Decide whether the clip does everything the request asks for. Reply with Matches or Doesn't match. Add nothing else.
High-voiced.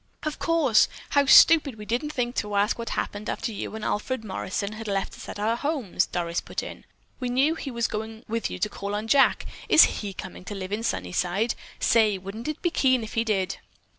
Matches